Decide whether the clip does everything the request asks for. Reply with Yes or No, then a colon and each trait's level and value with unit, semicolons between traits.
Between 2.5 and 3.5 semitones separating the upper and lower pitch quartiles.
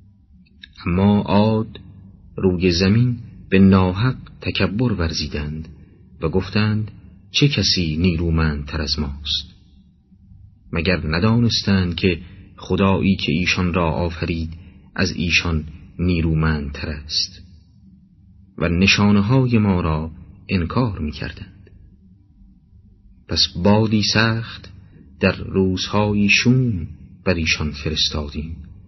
Yes: average, 3.1 semitones